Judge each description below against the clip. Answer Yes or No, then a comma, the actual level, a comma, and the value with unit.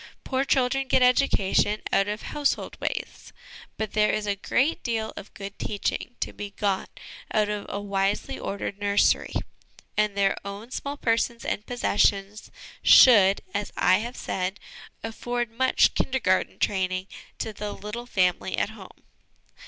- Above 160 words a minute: No, average, 145 wpm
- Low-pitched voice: No, high, 210 Hz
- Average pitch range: Yes, average, 3.2 semitones